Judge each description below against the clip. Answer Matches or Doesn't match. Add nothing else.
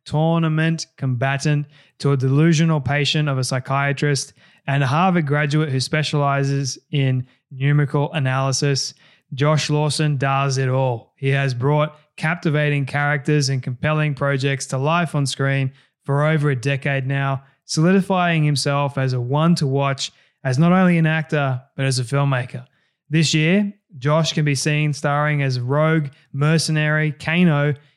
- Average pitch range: Doesn't match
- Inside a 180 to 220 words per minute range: Doesn't match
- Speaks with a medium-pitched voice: Matches